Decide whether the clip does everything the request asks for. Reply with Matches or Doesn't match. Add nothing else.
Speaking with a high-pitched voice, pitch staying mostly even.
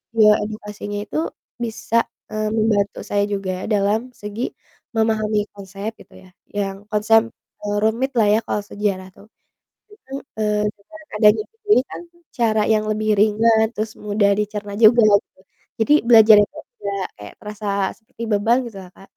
Matches